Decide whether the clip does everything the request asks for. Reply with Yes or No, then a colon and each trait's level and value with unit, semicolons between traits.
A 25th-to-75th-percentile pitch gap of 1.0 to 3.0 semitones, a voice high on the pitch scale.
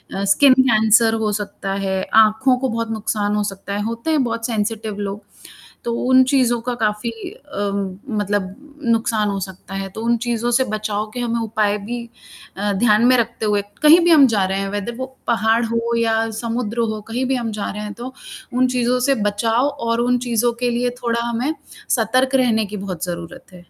Yes: average, 2.7 semitones; high, 230 Hz